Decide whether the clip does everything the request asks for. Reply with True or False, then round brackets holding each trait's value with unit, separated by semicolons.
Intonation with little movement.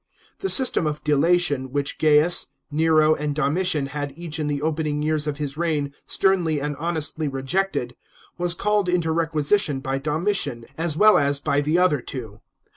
False (3.0 semitones)